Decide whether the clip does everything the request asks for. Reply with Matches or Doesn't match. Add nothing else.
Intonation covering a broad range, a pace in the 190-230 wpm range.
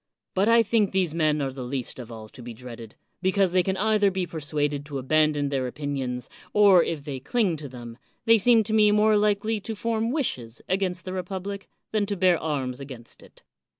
Matches